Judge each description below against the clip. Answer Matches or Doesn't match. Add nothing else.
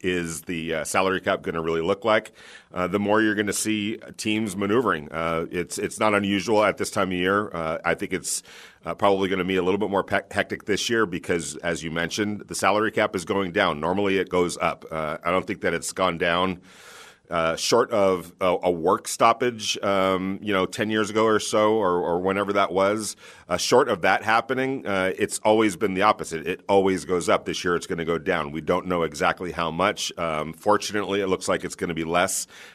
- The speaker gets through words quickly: Matches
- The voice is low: Matches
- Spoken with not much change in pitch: Doesn't match